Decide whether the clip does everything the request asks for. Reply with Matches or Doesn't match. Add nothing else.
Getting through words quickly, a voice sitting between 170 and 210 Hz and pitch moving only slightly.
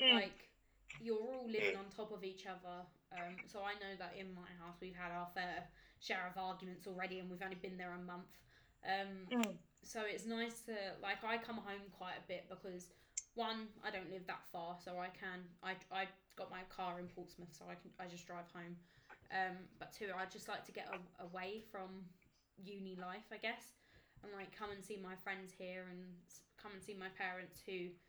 Matches